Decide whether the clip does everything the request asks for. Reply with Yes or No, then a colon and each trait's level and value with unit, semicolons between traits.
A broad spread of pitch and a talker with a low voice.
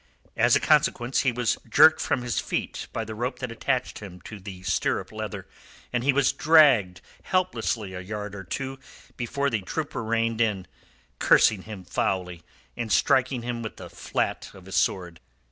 No: average, 4.7 semitones; low, 115 Hz